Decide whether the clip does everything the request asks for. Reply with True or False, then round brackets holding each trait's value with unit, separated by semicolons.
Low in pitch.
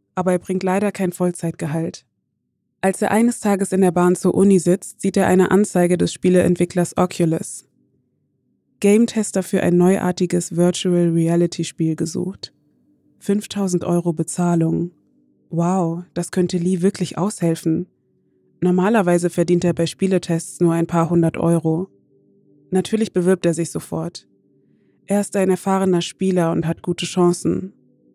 False (180 Hz)